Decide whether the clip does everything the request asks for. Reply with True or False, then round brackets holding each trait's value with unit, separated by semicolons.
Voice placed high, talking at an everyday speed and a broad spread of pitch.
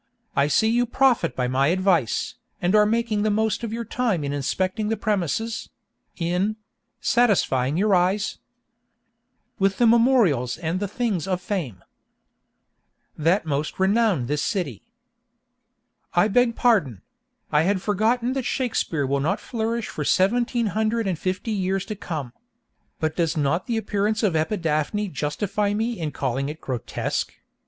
True (195 Hz; 145 wpm; 6.0 semitones)